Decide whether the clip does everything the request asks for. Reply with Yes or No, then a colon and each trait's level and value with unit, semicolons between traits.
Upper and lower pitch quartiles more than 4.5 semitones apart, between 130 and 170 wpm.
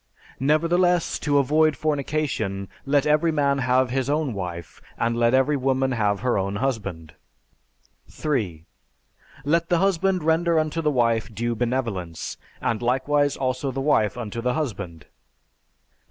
Yes: average, 4.9 semitones; average, 140 wpm